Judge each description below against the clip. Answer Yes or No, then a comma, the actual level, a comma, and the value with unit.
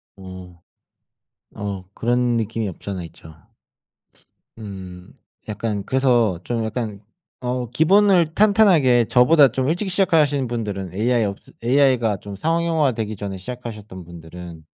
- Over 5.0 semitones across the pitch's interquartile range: Yes, wide, 5.5 semitones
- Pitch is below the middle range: Yes, low, 115 Hz